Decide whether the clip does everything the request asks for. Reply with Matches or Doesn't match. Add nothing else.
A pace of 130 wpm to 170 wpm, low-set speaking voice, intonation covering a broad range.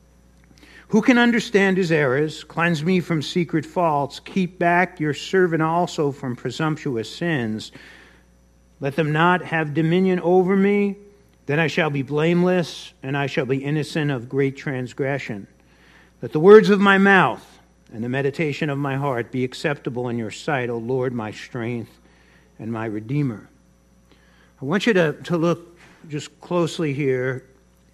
Doesn't match